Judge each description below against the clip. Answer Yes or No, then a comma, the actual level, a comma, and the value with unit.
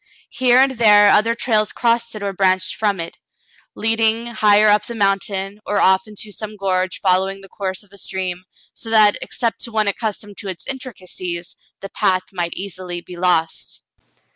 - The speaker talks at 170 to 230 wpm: Yes, average, 175 wpm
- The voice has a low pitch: No, high, 200 Hz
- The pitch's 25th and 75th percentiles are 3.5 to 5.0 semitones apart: No, average, 2.7 semitones